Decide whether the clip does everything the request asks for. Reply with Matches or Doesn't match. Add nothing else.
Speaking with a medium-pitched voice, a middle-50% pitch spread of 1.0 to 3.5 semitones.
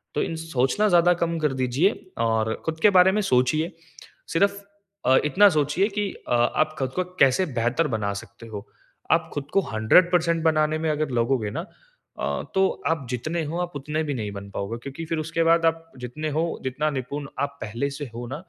Doesn't match